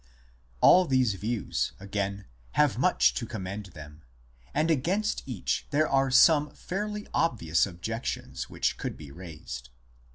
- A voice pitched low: Yes, low, 115 Hz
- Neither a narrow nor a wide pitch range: No, wide, 8.1 semitones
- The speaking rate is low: Yes, slow, 130 wpm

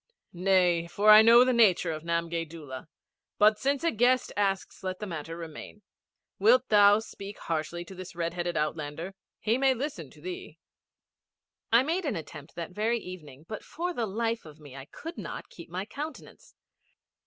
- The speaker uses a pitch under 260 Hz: Yes, medium, 185 Hz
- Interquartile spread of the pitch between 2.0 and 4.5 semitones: No, wide, 5.5 semitones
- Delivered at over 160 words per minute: Yes, average, 175 wpm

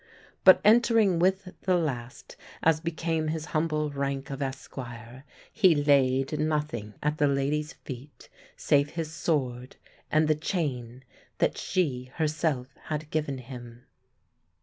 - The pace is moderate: No, slow, 125 wpm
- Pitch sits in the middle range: Yes, medium, 150 Hz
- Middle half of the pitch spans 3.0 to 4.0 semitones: Yes, average, 3.4 semitones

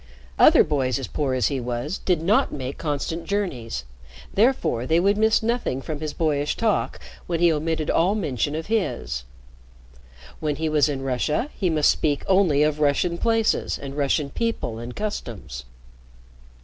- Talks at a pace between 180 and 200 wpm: No, average, 160 wpm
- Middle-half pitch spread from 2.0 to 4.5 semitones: No, wide, 5.5 semitones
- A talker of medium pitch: Yes, medium, 155 Hz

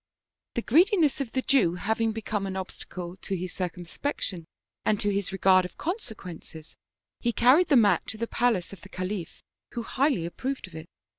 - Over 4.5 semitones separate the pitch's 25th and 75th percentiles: Yes, average, 5.2 semitones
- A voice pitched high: Yes, high, 205 Hz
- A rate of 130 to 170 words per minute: No, average, 180 wpm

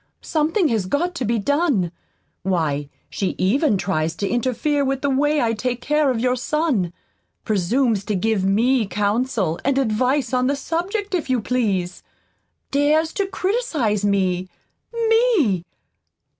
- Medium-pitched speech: No, very high, 250 Hz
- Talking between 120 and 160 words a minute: Yes, average, 145 wpm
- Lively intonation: Yes, wide, 6.7 semitones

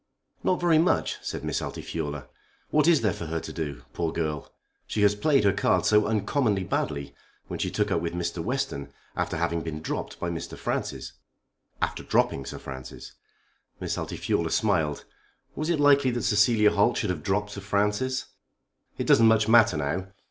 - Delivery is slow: No, average, 175 wpm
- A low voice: Yes, low, 100 Hz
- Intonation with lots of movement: Yes, wide, 5.8 semitones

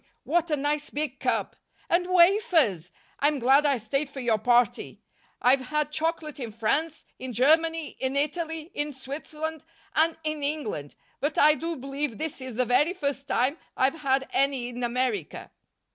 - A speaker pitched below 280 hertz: No, very high, 285 Hz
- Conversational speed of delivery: Yes, average, 160 wpm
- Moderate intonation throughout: Yes, average, 3.6 semitones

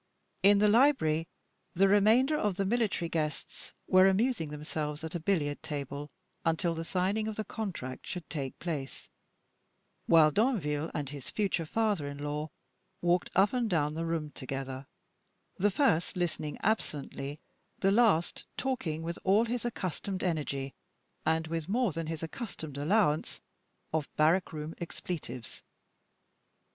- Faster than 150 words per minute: No, average, 140 wpm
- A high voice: No, medium, 165 Hz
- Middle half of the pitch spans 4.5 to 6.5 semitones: Yes, average, 5.2 semitones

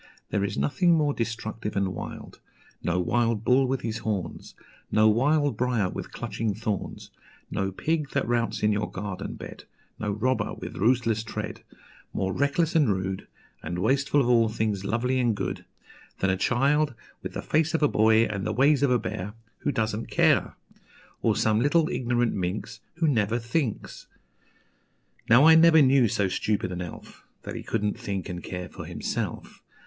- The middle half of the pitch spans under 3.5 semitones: No, average, 4.8 semitones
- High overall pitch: No, low, 115 Hz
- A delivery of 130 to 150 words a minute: No, average, 175 wpm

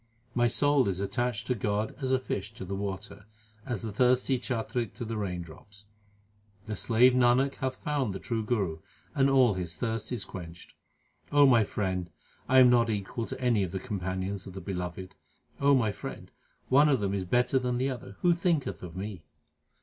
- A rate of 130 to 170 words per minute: No, average, 190 wpm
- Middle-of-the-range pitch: No, low, 110 Hz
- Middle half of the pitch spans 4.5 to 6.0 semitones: Yes, average, 4.8 semitones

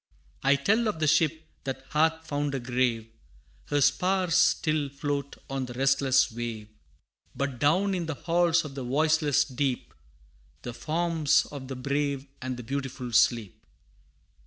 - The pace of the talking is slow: No, average, 150 wpm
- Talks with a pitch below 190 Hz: Yes, medium, 140 Hz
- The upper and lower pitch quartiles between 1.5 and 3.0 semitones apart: No, average, 3.5 semitones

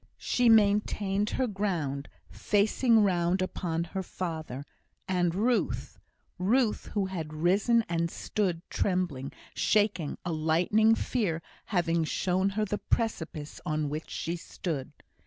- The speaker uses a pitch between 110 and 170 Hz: No, medium, 185 Hz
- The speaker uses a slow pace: Yes, slow, 120 wpm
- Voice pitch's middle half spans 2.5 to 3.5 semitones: No, average, 4.2 semitones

